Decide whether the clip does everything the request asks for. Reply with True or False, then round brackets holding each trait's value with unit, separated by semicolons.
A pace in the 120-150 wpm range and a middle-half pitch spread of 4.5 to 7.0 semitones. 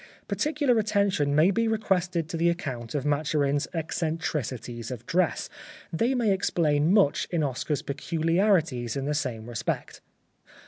True (140 wpm; 5.1 semitones)